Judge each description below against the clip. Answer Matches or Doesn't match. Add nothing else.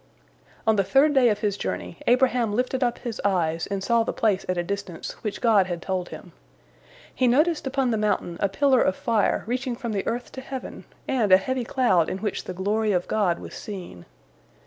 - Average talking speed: Doesn't match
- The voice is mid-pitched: Doesn't match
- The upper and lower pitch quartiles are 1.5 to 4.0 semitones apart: Doesn't match